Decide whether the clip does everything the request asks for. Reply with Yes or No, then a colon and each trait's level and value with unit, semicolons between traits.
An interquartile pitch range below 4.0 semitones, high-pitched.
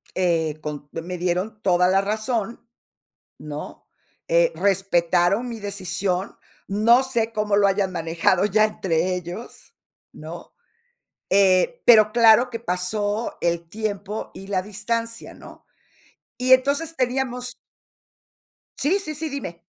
No: average, 4.5 semitones; high, 205 Hz